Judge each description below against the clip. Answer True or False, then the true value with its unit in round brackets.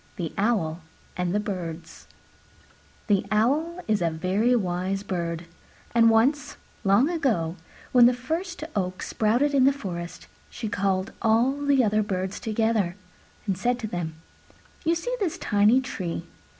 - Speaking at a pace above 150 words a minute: False (145 wpm)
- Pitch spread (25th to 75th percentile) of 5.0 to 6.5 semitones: True (5.5 semitones)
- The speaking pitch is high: True (215 Hz)